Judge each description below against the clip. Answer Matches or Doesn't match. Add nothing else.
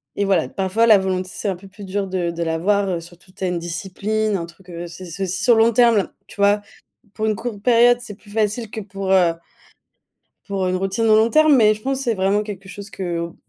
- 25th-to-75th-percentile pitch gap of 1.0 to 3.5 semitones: Matches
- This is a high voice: Matches